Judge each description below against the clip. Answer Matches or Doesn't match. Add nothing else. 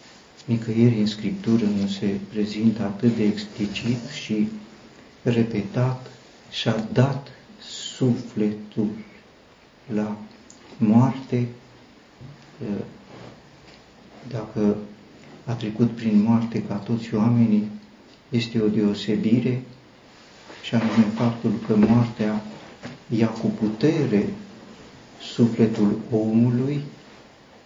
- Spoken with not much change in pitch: Matches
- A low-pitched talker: Matches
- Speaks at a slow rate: Matches